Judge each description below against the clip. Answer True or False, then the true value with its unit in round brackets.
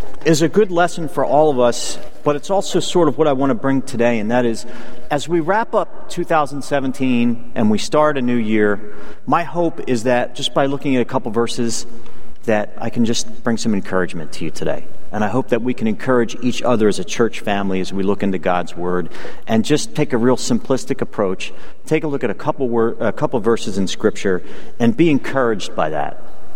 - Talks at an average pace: False (215 wpm)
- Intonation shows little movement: False (4.9 semitones)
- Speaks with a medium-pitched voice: False (120 Hz)